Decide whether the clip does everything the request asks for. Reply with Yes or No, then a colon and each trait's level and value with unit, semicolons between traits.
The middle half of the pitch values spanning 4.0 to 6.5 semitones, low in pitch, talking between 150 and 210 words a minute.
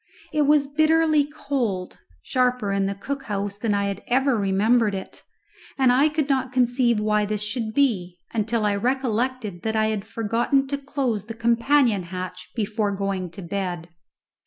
No: average, 4.7 semitones; high, 225 Hz; average, 165 wpm